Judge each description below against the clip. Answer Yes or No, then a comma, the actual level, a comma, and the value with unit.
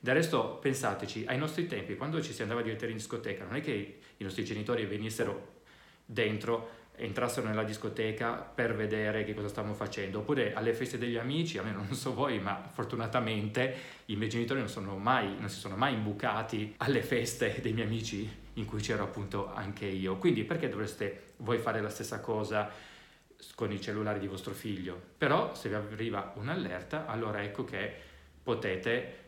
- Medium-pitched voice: No, low, 110 Hz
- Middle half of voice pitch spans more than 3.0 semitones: No, narrow, 2.4 semitones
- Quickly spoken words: Yes, fast, 180 wpm